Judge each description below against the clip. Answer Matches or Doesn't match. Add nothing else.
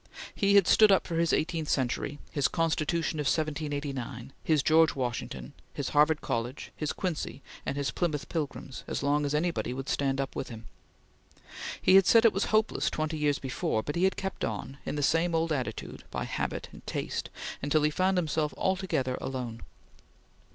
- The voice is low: Doesn't match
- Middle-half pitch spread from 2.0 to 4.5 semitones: Matches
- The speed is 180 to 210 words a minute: Matches